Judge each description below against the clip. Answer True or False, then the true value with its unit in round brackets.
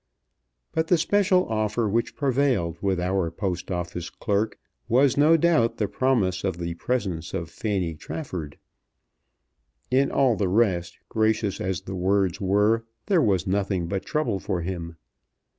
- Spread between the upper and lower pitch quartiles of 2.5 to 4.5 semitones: False (5.2 semitones)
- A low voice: True (100 Hz)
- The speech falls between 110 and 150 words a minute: True (145 wpm)